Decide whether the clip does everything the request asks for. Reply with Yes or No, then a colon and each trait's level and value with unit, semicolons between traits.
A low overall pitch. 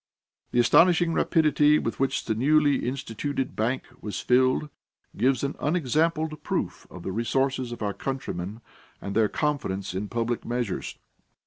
Yes: low, 130 Hz